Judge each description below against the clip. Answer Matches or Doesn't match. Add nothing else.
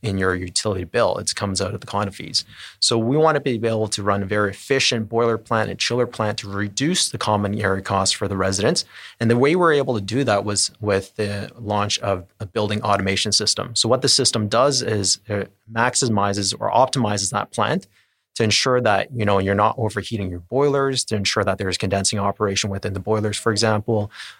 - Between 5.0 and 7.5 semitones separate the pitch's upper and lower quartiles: Doesn't match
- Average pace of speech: Doesn't match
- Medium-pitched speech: Doesn't match